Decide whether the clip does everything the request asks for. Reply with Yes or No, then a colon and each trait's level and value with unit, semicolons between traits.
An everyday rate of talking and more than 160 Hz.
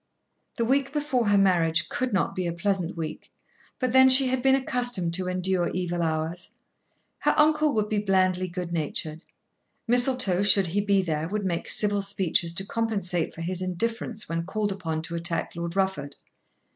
Yes: average, 175 wpm; high, 190 Hz